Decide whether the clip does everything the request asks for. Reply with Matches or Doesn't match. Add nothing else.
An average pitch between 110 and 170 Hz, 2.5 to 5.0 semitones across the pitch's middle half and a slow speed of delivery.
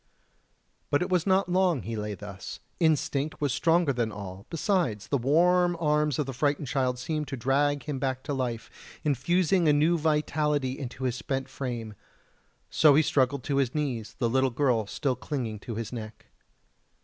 Doesn't match